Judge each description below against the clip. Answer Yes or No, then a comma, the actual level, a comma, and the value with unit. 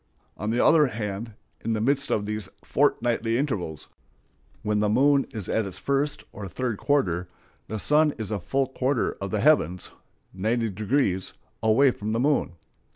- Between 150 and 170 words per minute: Yes, average, 160 wpm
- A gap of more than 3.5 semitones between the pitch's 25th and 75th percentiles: Yes, average, 4.9 semitones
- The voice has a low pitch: Yes, low, 110 Hz